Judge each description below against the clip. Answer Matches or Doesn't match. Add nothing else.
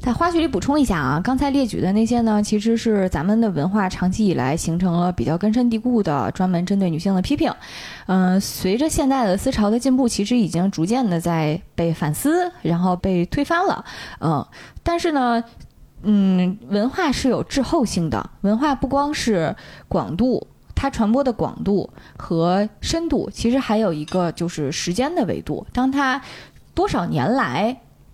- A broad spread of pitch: Matches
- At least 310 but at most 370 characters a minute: Doesn't match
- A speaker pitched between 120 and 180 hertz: Doesn't match